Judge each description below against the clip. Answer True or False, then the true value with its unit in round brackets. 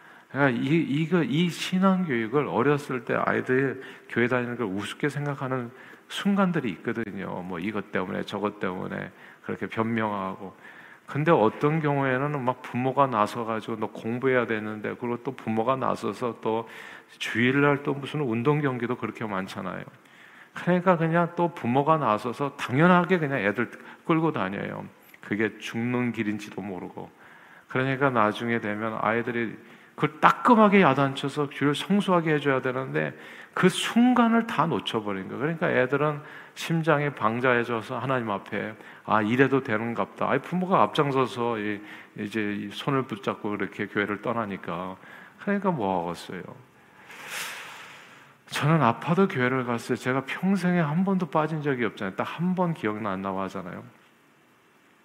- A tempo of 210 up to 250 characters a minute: False (325 characters per minute)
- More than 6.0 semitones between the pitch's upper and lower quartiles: False (5.5 semitones)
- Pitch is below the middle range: True (125 Hz)